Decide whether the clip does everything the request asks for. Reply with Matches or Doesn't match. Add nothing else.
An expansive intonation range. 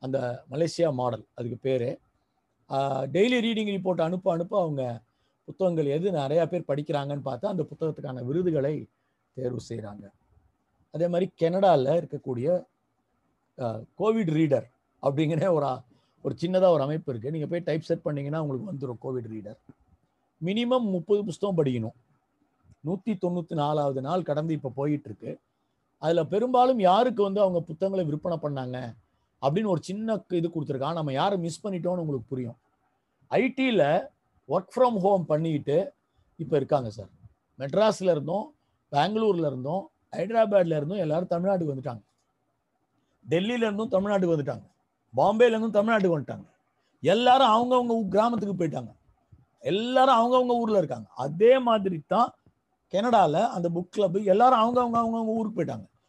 Matches